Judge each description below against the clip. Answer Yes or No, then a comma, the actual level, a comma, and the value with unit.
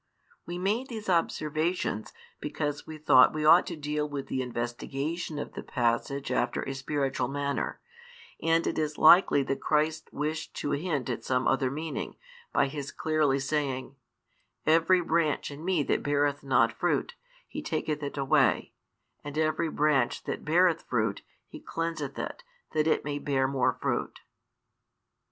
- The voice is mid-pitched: Yes, medium, 150 Hz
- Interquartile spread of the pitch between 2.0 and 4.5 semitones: Yes, average, 2.7 semitones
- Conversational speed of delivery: Yes, average, 155 wpm